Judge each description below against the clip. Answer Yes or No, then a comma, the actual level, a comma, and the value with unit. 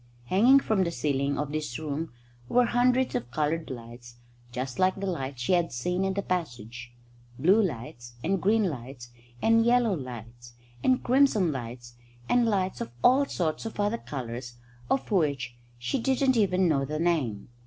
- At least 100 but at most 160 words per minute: No, average, 170 wpm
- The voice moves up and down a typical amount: No, wide, 8.8 semitones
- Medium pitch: Yes, medium, 160 Hz